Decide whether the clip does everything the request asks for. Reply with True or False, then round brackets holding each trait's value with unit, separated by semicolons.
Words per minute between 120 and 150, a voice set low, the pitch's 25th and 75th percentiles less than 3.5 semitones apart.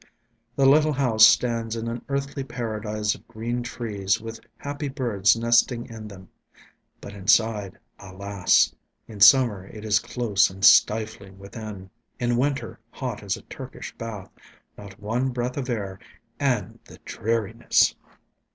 True (140 wpm; 115 Hz; 3.1 semitones)